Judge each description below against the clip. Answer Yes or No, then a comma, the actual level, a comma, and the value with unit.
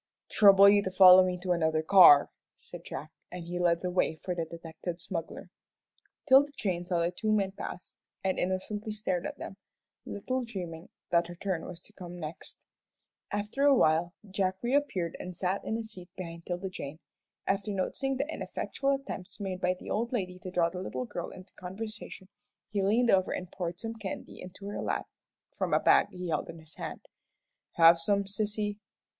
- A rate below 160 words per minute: No, average, 185 wpm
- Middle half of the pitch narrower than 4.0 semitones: Yes, average, 3.0 semitones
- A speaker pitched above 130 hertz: Yes, medium, 185 Hz